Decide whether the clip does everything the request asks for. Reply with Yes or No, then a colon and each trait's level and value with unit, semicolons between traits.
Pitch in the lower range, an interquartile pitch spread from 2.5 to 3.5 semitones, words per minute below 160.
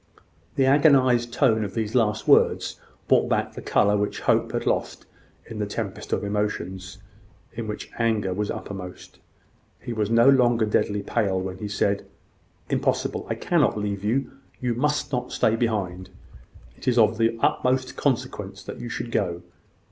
No: low, 110 Hz; average, 2.9 semitones; average, 165 wpm